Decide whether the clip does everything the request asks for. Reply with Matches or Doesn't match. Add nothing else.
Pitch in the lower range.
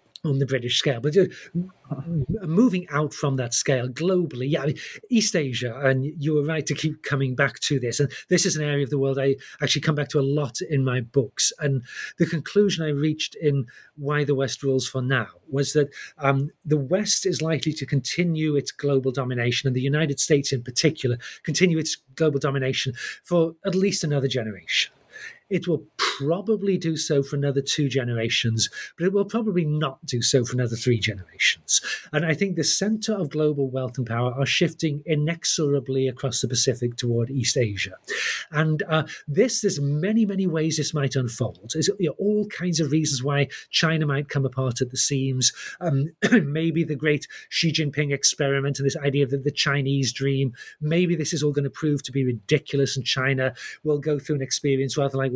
Doesn't match